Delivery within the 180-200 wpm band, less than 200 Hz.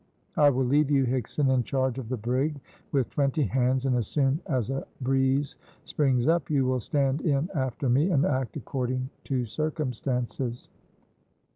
No: average, 165 wpm; low, 135 Hz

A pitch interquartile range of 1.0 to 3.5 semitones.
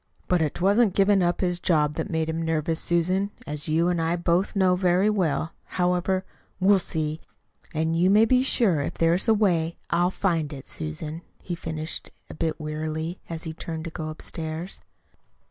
Yes: average, 2.7 semitones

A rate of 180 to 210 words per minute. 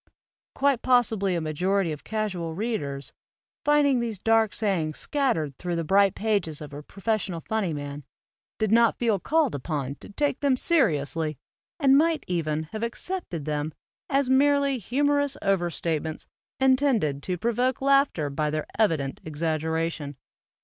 No: average, 145 wpm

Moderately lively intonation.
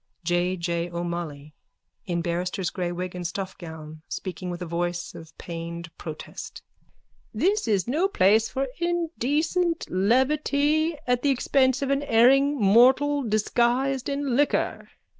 No: wide, 8.1 semitones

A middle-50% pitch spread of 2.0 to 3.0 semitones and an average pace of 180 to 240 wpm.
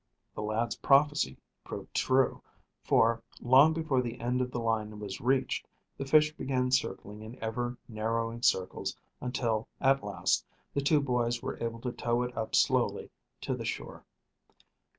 No: average, 2.7 semitones; average, 155 wpm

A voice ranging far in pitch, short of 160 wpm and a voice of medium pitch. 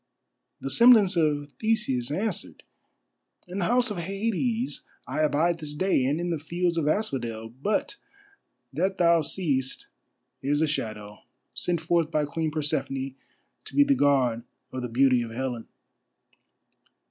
Yes: wide, 5.8 semitones; average, 145 wpm; medium, 155 Hz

